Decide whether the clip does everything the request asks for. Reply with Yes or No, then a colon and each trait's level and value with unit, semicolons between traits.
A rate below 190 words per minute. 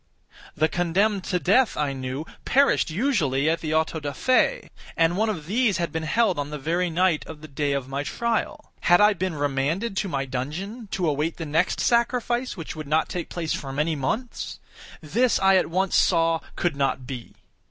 No: average, 195 wpm